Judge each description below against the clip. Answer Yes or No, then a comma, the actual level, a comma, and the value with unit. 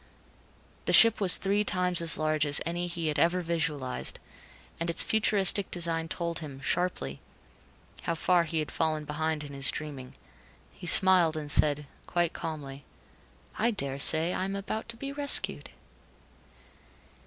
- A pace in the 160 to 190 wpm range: No, average, 150 wpm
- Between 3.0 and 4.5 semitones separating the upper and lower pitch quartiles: Yes, average, 3.3 semitones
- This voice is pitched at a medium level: Yes, medium, 165 Hz